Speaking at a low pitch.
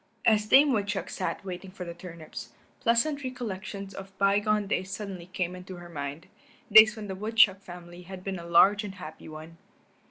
No: high, 190 Hz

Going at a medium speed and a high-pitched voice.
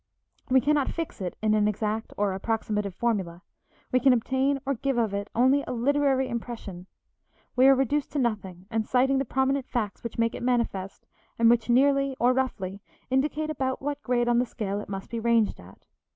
Yes: average, 195 wpm; high, 240 Hz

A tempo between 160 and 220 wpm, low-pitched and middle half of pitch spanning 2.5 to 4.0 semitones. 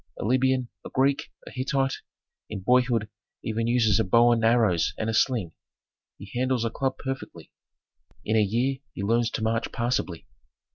Yes: average, 170 wpm; low, 115 Hz; average, 2.8 semitones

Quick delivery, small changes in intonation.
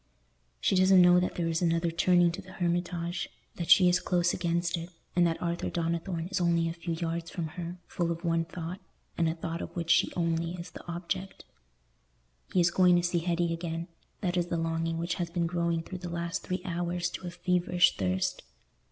Yes: fast, 210 wpm; narrow, 1.1 semitones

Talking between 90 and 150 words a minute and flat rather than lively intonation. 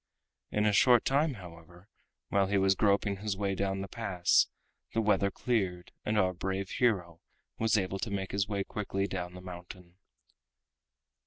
No: average, 165 wpm; narrow, 2.3 semitones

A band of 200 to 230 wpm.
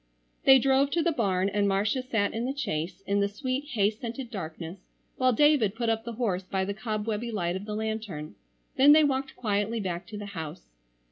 Yes: fast, 205 wpm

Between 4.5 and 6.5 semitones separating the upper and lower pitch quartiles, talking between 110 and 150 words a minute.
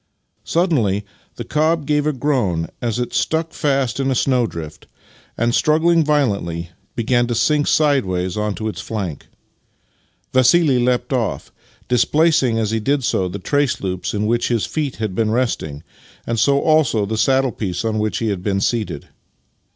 No: average, 5.3 semitones; average, 160 wpm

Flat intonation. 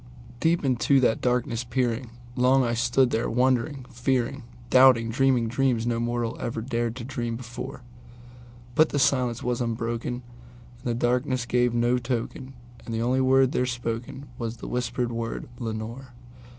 Yes: narrow, 1.6 semitones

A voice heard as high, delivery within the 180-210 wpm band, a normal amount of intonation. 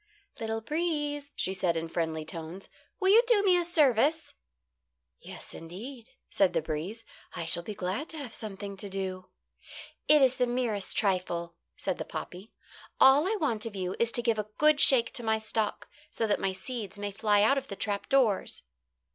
No: high, 220 Hz; average, 190 wpm; wide, 6.3 semitones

